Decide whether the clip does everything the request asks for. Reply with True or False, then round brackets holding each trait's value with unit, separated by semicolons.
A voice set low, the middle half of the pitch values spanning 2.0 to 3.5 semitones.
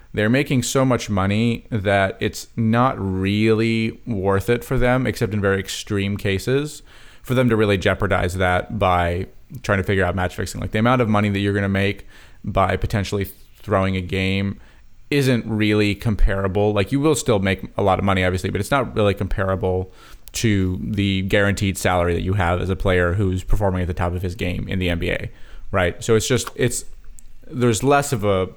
True (100 Hz; 3.1 semitones)